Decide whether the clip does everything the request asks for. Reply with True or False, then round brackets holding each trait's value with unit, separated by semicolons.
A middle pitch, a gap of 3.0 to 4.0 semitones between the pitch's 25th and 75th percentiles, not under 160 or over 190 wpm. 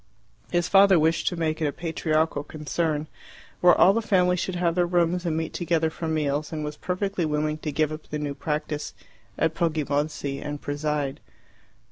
False (160 Hz; 2.5 semitones; 180 wpm)